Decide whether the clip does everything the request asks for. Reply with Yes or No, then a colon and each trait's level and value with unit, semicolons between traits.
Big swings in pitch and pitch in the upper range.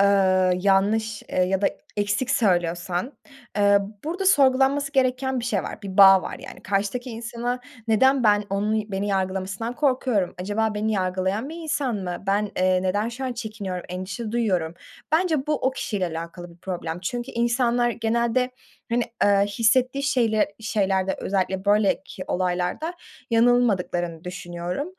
No: average, 4.6 semitones; high, 210 Hz